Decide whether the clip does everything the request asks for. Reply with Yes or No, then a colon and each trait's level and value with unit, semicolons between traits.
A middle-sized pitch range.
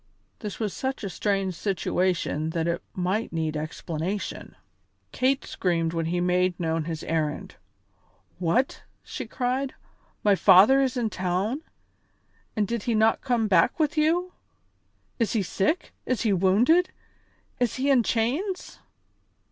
No: wide, 6.2 semitones